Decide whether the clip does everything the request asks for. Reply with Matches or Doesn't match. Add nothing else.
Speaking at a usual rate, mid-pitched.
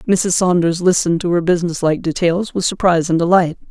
Matches